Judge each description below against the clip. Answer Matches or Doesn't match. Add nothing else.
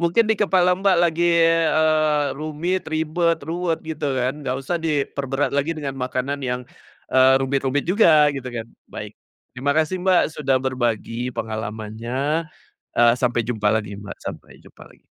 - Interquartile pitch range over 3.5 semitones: Matches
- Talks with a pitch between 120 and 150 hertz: Matches